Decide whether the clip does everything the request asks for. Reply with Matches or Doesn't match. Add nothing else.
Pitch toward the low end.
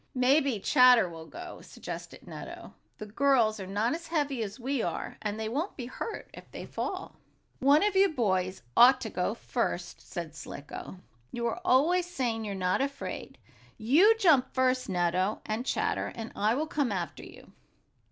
Doesn't match